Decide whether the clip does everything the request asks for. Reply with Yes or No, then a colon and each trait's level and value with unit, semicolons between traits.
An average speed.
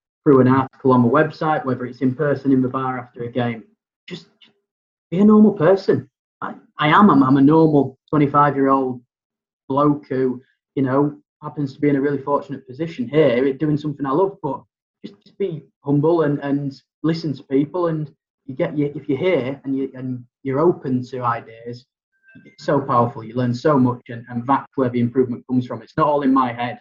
No: fast, 210 wpm